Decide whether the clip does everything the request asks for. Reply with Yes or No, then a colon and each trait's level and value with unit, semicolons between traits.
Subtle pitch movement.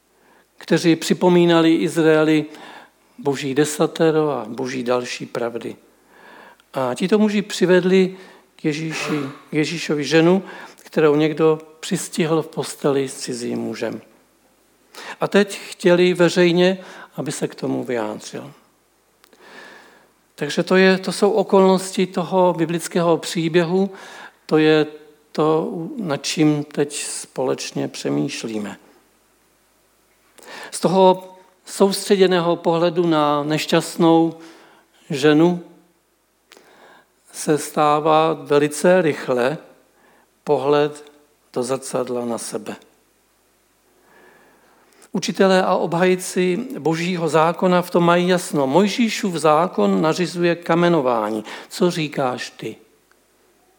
No: average, 3.5 semitones